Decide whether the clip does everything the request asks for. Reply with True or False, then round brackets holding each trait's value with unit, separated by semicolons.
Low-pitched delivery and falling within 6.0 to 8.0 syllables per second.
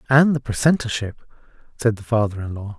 True (115 Hz; 6.2 syllables/s)